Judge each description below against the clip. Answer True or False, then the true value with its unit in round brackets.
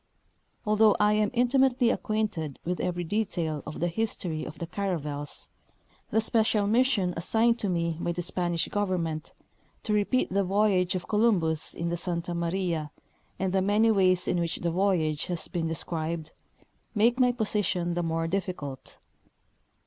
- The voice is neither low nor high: True (180 Hz)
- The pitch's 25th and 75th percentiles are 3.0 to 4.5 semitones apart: True (4.0 semitones)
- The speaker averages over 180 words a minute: False (155 wpm)